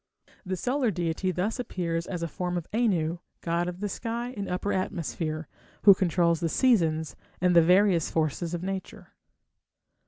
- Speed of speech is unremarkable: Yes, average, 160 wpm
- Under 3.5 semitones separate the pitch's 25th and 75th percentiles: Yes, average, 3.0 semitones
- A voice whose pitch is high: No, medium, 180 Hz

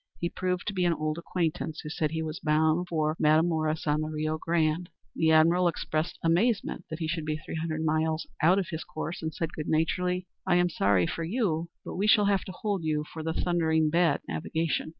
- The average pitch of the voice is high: No, medium, 160 Hz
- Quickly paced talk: Yes, fast, 215 wpm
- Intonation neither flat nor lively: No, narrow, 2.1 semitones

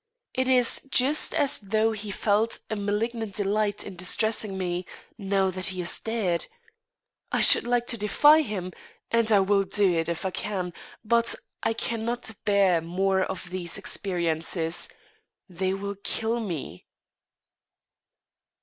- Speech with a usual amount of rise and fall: Yes, average, 3.3 semitones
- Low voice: No, high, 200 Hz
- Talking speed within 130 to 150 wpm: Yes, average, 140 wpm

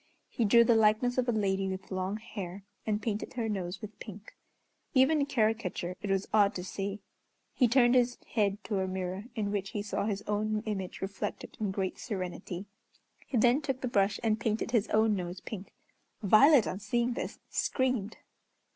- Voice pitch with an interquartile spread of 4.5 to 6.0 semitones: No, average, 3.2 semitones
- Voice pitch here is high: Yes, high, 210 Hz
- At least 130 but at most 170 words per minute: No, average, 185 wpm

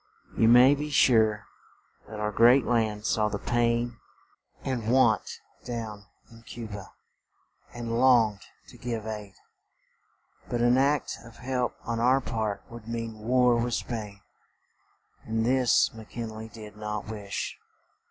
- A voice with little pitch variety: Yes, narrow, 2.1 semitones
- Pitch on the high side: No, low, 115 Hz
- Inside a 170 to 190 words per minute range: No, average, 145 wpm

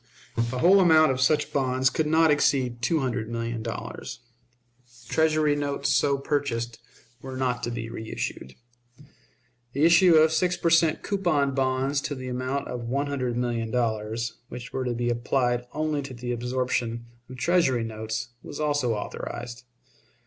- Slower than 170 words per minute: Yes, average, 155 wpm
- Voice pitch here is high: No, low, 130 Hz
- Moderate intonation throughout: Yes, average, 3.7 semitones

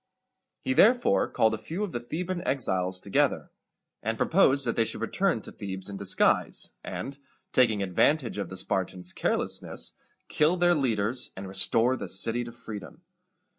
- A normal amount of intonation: No, wide, 6.8 semitones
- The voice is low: Yes, low, 115 Hz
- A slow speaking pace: No, average, 160 wpm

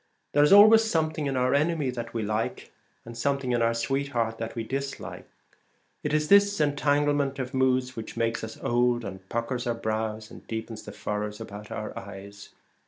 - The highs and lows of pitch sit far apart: No, average, 4.1 semitones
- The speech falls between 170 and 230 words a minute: Yes, average, 180 wpm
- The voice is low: Yes, low, 120 Hz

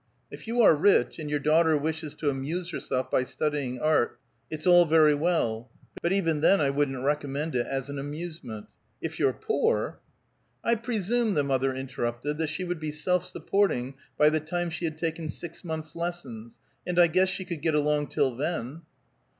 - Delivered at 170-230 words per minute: Yes, average, 190 wpm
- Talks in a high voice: No, medium, 155 Hz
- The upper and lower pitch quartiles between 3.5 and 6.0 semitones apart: Yes, average, 3.8 semitones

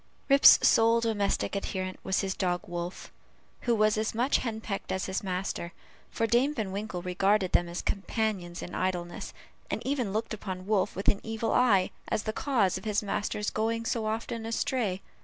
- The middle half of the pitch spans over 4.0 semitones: No, average, 3.2 semitones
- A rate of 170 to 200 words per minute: Yes, average, 175 wpm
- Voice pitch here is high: Yes, high, 210 Hz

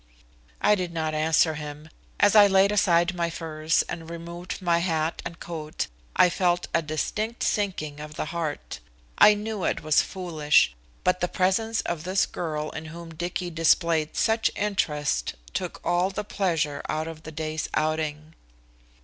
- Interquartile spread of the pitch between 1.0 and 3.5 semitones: Yes, average, 2.9 semitones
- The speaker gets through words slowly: No, average, 160 wpm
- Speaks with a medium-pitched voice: Yes, medium, 170 Hz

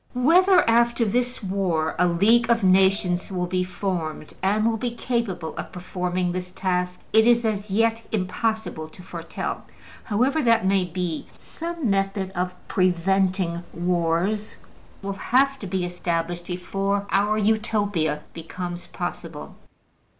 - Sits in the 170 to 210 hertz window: Yes, high, 190 Hz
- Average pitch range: Yes, average, 3.8 semitones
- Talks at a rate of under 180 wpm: Yes, slow, 135 wpm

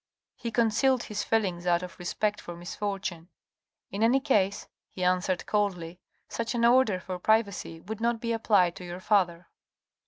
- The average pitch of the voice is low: No, high, 200 Hz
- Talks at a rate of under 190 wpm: Yes, average, 175 wpm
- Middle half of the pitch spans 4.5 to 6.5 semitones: No, average, 3.9 semitones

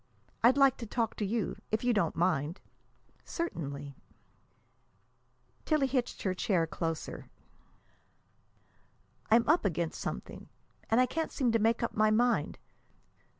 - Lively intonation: Yes, wide, 6.1 semitones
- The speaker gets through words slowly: Yes, slow, 130 wpm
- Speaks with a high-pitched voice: Yes, high, 225 Hz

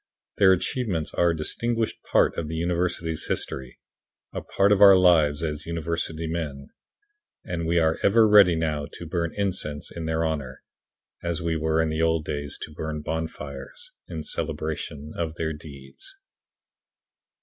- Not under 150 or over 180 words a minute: Yes, average, 155 wpm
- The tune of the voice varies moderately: No, narrow, 2.1 semitones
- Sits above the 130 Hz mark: No, very low, 80 Hz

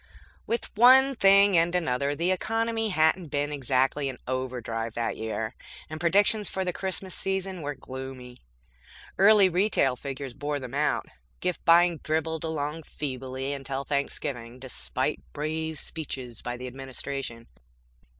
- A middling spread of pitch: No, wide, 5.7 semitones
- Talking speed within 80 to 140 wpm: Yes, slow, 135 wpm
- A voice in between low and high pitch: Yes, medium, 145 Hz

